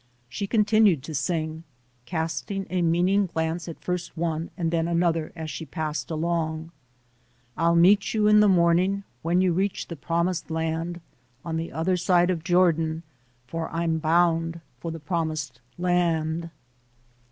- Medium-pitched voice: Yes, medium, 170 Hz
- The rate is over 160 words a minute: No, average, 150 wpm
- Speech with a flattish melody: Yes, narrow, 1.8 semitones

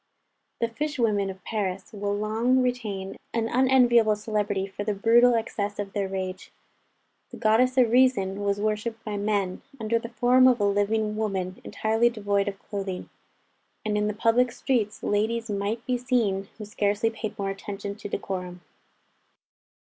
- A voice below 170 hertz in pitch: No, high, 215 Hz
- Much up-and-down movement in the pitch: No, narrow, 2.5 semitones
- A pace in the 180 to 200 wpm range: No, average, 160 wpm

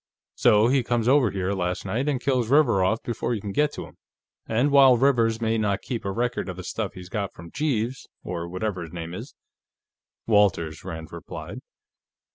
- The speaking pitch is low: Yes, low, 110 Hz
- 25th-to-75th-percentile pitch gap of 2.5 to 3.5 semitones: No, average, 4.9 semitones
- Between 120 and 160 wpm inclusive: No, average, 200 wpm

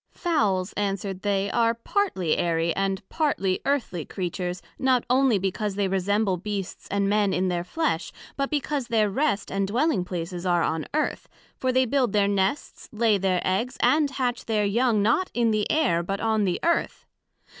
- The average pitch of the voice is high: Yes, high, 205 Hz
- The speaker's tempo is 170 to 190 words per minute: Yes, average, 175 wpm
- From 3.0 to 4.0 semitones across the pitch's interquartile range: No, average, 4.8 semitones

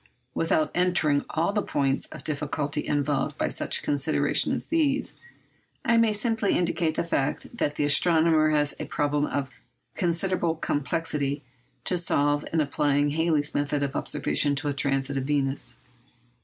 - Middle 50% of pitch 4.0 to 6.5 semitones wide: No, average, 2.7 semitones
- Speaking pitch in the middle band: Yes, medium, 150 Hz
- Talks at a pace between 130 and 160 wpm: Yes, average, 155 wpm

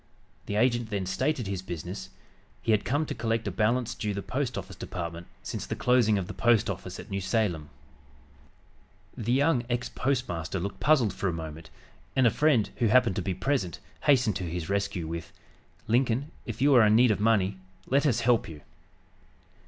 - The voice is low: Yes, low, 110 Hz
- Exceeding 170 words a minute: Yes, average, 190 wpm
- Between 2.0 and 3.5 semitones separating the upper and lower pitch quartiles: No, average, 5.0 semitones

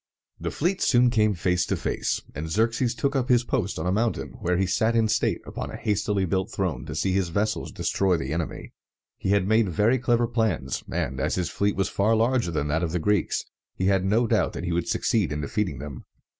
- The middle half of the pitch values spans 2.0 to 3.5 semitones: No, average, 4.5 semitones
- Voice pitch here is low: Yes, low, 100 Hz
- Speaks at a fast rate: Yes, fast, 225 wpm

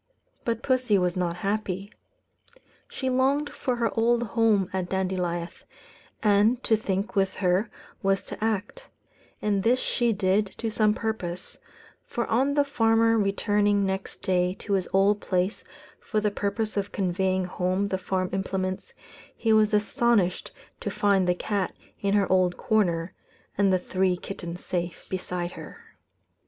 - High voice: Yes, high, 200 Hz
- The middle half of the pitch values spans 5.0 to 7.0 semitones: No, average, 3.0 semitones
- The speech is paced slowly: No, average, 150 wpm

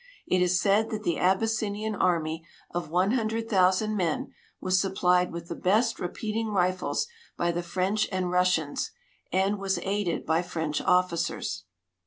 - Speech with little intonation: No, average, 3.0 semitones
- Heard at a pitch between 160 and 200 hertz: Yes, medium, 185 Hz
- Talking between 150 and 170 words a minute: Yes, average, 155 wpm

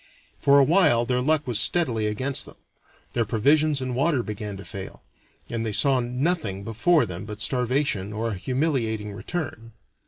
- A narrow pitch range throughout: No, average, 4.9 semitones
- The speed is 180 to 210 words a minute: No, average, 165 wpm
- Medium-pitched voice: No, low, 120 Hz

